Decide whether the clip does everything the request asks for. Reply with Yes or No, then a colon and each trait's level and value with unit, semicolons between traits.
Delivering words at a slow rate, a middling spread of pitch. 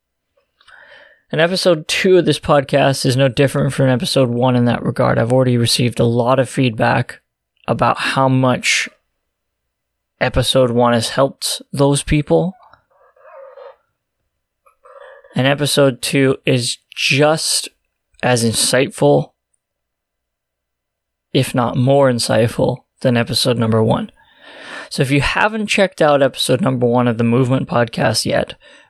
Yes: slow, 125 wpm; average, 3.7 semitones